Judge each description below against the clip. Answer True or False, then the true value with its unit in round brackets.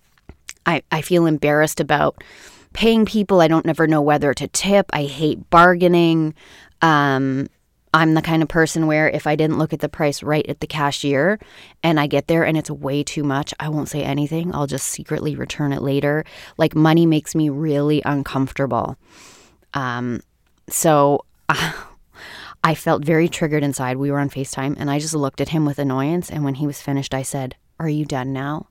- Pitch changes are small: True (2.3 semitones)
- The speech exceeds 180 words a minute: True (190 wpm)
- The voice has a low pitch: False (150 Hz)